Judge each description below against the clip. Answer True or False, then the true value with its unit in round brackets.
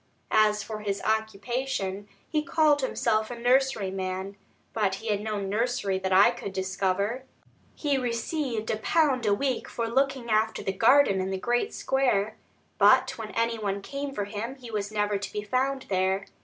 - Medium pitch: False (220 Hz)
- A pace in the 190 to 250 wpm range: False (170 wpm)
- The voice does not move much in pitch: False (4.2 semitones)